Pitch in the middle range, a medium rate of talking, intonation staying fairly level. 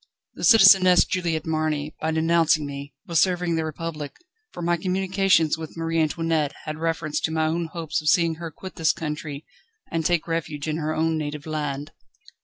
Yes: medium, 160 Hz; average, 180 wpm; narrow, 1.7 semitones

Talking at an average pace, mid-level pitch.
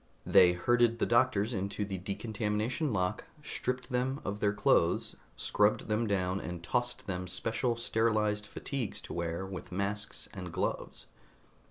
No: average, 145 wpm; low, 105 Hz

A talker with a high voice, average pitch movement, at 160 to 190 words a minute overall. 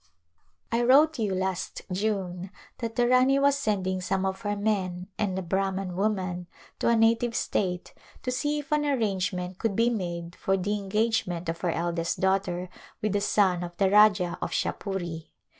Yes: high, 195 Hz; average, 3.7 semitones; average, 175 wpm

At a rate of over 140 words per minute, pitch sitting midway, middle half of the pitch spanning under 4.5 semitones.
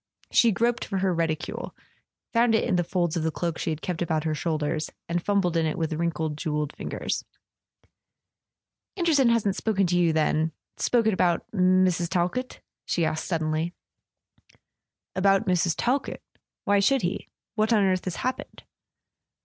Yes: average, 155 wpm; medium, 175 Hz; average, 3.9 semitones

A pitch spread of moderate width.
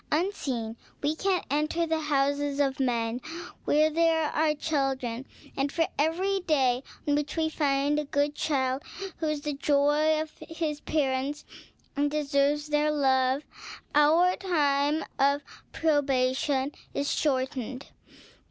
No: narrow, 2.2 semitones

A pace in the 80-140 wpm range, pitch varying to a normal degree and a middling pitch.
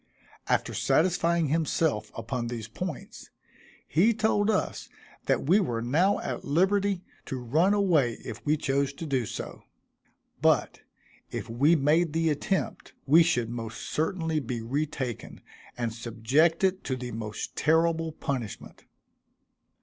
No: slow, 135 wpm; wide, 5.7 semitones; medium, 150 Hz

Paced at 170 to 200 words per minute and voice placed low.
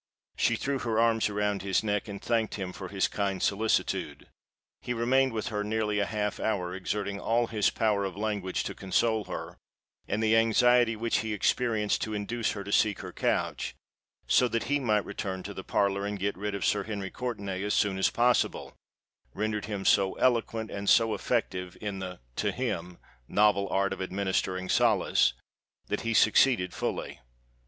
Yes: average, 180 wpm; low, 105 Hz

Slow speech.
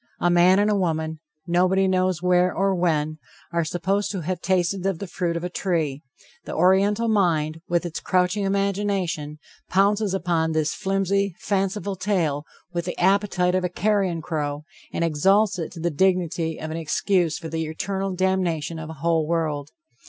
No: average, 175 wpm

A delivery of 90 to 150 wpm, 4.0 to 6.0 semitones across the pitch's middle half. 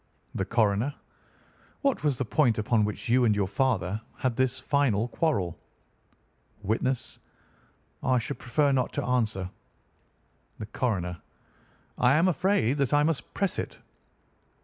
Yes: slow, 135 wpm; average, 4.9 semitones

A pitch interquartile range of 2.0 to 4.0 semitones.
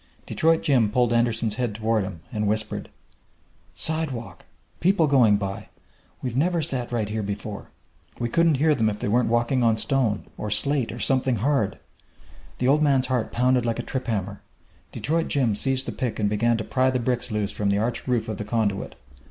Yes: average, 3.7 semitones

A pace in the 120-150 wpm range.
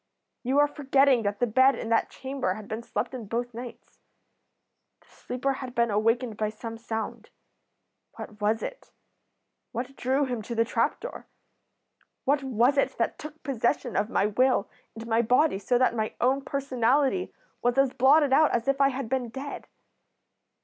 No: average, 175 wpm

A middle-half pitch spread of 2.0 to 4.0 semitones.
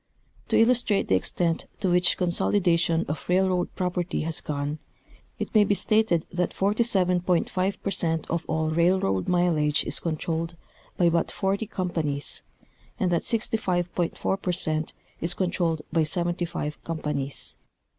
Yes: narrow, 2.6 semitones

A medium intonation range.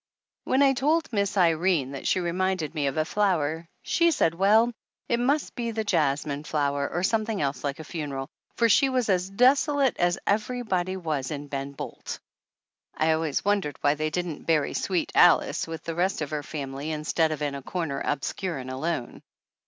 No: wide, 5.8 semitones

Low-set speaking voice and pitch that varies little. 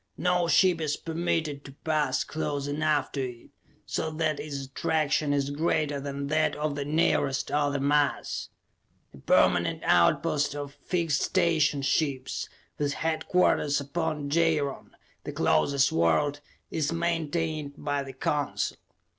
No: medium, 145 Hz; narrow, 2.0 semitones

